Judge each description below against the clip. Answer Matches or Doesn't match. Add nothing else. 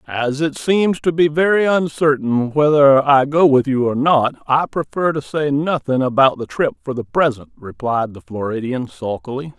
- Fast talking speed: Doesn't match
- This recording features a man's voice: Matches